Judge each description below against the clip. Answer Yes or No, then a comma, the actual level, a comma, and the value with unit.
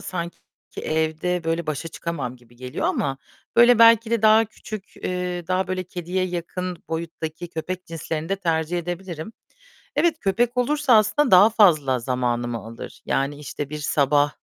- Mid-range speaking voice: Yes, medium, 170 Hz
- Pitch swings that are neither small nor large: Yes, average, 4.3 semitones